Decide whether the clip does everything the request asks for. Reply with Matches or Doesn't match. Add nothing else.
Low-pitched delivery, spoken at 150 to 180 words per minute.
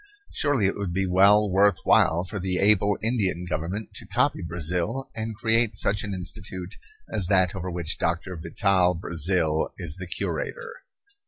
Matches